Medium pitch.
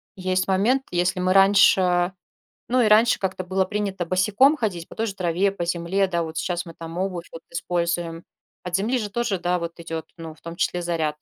Yes: medium, 180 Hz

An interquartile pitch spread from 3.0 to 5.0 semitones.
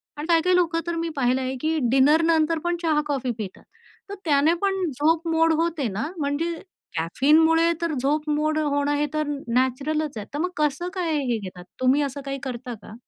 Yes: average, 3.4 semitones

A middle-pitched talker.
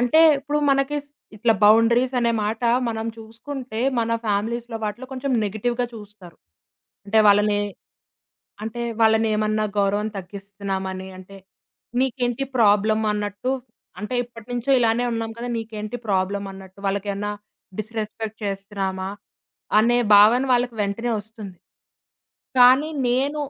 No: high, 220 Hz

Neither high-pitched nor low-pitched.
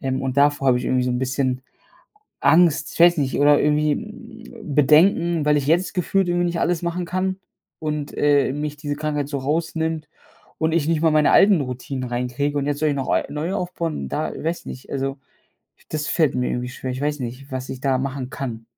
Yes: medium, 145 Hz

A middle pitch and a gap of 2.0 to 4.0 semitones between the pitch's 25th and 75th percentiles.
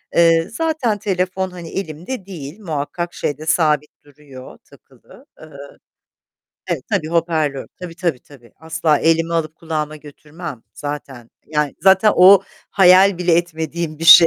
Yes: medium, 165 Hz; average, 3.2 semitones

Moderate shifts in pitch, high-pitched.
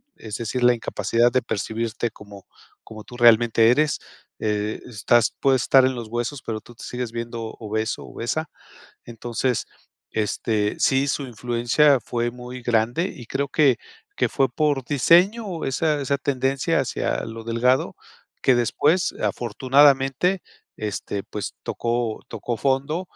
No: average, 3.1 semitones; low, 120 Hz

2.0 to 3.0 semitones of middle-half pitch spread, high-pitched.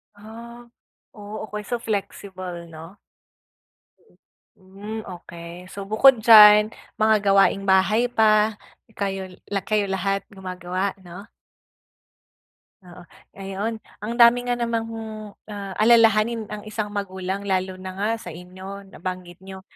Yes: narrow, 2.5 semitones; high, 200 Hz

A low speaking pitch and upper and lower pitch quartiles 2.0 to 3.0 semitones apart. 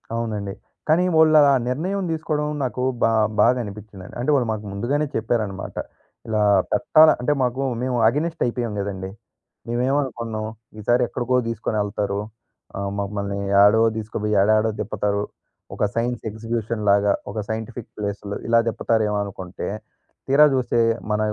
No: low, 115 Hz; average, 3.5 semitones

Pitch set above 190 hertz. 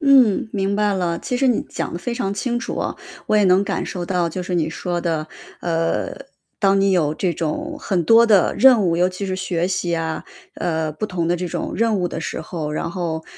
No: medium, 185 Hz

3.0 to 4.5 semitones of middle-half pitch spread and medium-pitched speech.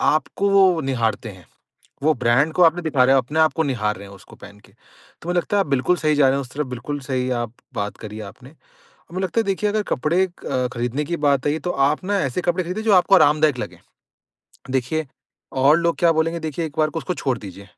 No: average, 5.2 semitones; medium, 145 Hz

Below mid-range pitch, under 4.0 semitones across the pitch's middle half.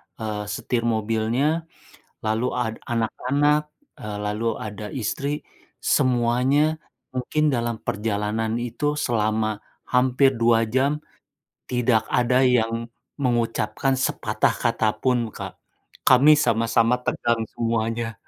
Yes: low, 120 Hz; narrow, 2.6 semitones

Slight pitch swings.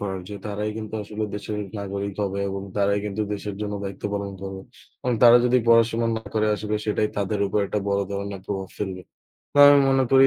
Yes: narrow, 1.5 semitones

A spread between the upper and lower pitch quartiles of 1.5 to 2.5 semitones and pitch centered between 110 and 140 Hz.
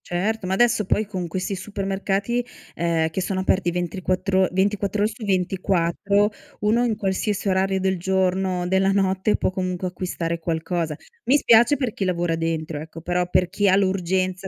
No: narrow, 2.1 semitones; high, 190 Hz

